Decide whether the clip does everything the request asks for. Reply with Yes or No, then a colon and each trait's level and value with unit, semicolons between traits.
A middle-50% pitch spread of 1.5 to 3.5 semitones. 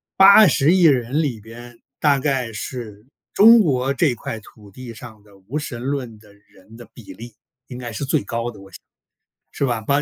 No: average, 3.9 semitones